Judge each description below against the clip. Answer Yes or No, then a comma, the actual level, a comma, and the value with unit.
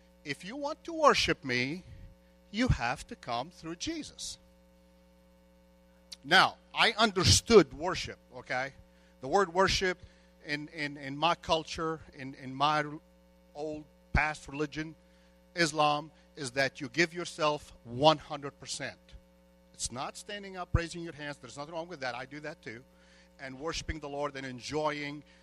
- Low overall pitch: No, medium, 145 Hz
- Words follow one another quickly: No, average, 140 wpm